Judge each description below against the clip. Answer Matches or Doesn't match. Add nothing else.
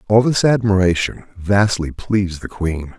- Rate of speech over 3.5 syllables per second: Matches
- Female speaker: Doesn't match